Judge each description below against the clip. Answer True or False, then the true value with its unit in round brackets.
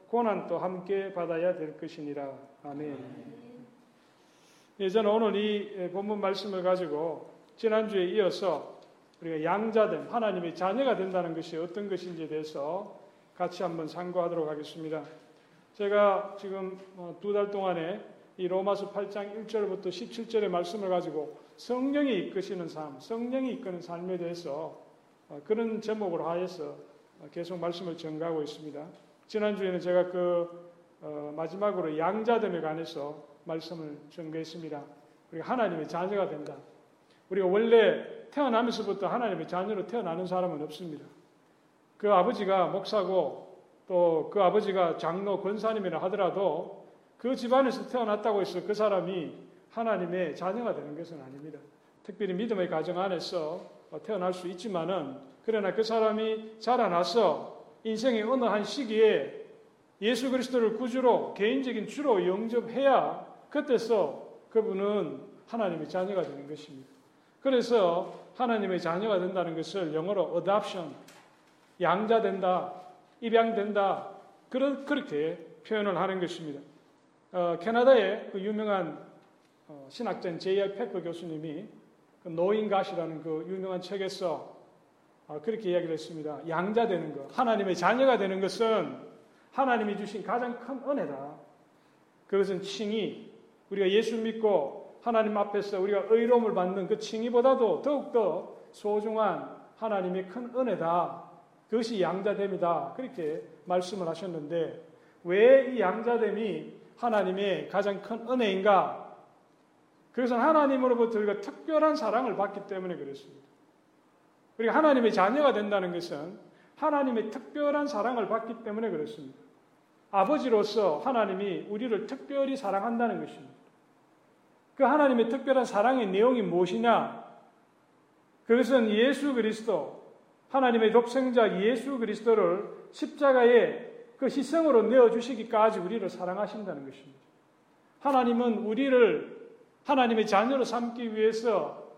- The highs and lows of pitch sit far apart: False (4.7 semitones)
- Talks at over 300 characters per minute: True (310 characters per minute)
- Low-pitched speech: False (200 Hz)